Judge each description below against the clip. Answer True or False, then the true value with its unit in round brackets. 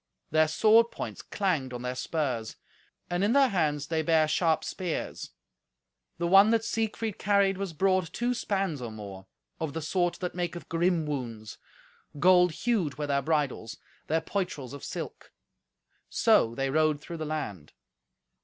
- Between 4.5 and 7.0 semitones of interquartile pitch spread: True (5.0 semitones)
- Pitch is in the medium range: True (160 Hz)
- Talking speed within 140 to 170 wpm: True (155 wpm)